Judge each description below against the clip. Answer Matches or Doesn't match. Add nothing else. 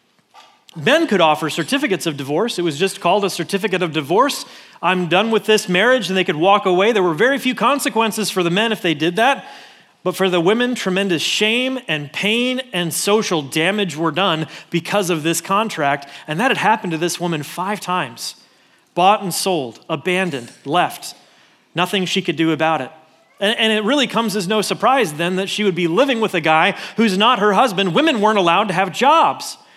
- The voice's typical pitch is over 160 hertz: Matches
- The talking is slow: Doesn't match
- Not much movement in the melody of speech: Doesn't match